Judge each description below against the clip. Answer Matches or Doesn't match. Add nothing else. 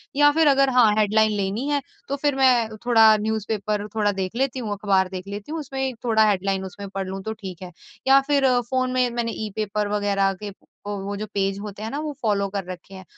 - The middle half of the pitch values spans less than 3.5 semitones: Doesn't match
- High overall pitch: Matches